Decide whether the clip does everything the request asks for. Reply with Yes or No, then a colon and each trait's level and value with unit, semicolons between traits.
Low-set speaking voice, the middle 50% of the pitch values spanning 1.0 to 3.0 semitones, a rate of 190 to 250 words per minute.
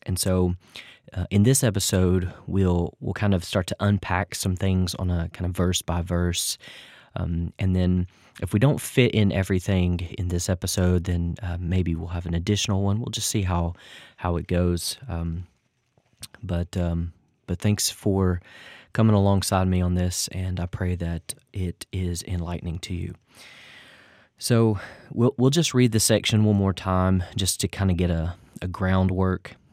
No: very low, 95 Hz; narrow, 2.5 semitones; average, 175 wpm